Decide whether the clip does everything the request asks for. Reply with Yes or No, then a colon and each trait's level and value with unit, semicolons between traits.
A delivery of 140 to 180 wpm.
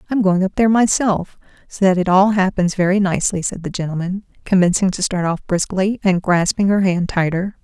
No: average, 195 wpm